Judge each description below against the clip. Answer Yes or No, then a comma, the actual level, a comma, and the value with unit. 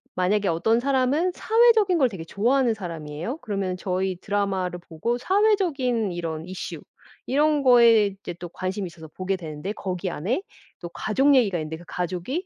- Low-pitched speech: No, high, 200 Hz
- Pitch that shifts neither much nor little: No, wide, 6.7 semitones